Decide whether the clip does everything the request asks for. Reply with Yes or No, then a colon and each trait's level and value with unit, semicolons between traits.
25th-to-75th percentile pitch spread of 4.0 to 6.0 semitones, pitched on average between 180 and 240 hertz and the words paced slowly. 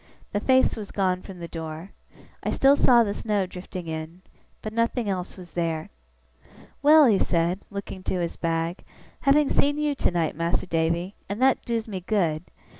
No: average, 5.3 semitones; medium, 185 Hz; average, 175 wpm